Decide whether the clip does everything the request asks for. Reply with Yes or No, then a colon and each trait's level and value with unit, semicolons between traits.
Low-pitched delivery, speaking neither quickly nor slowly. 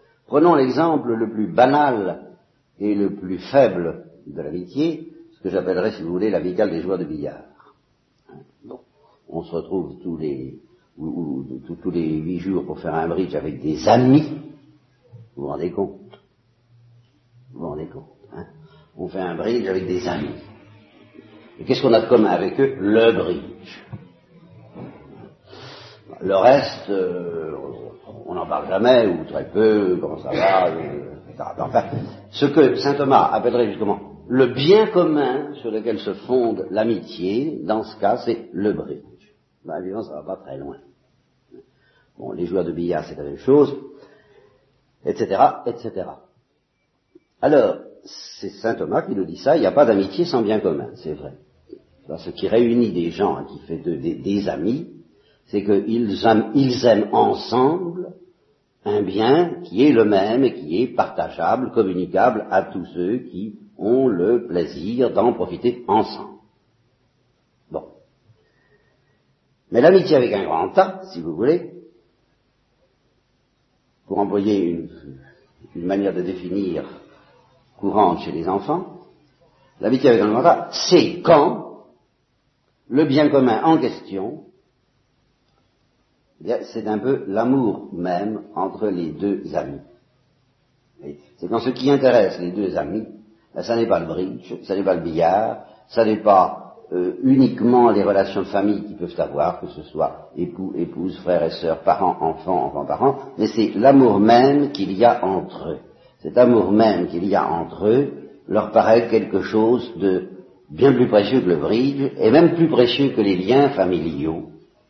Yes: low, 115 Hz; average, 160 wpm